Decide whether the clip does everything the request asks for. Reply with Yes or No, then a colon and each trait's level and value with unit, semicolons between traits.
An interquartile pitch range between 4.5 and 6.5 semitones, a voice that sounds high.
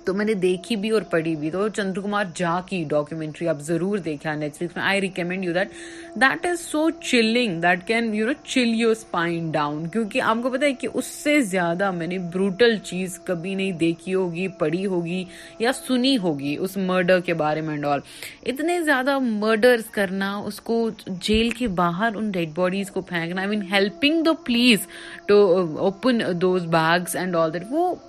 Yes: average, 5.0 semitones; high, 195 Hz